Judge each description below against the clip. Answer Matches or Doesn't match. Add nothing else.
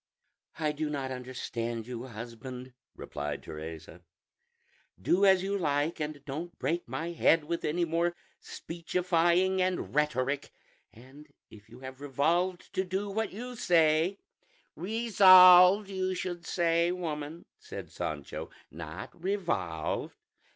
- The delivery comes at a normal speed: Doesn't match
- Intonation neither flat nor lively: Doesn't match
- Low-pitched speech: Doesn't match